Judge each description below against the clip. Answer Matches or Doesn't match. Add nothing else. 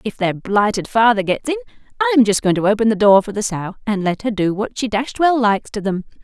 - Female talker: Matches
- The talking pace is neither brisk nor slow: Doesn't match